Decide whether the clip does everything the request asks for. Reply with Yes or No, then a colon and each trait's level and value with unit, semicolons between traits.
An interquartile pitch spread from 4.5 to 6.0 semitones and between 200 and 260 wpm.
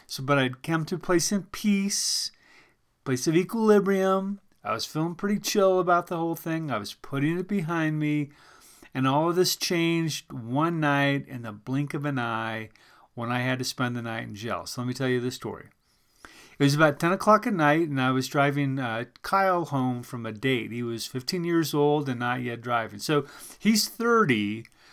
Yes: wide, 5.5 semitones; fast, 205 wpm